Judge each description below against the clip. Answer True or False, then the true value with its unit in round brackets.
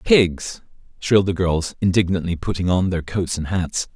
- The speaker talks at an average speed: True (165 wpm)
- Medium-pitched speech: False (90 Hz)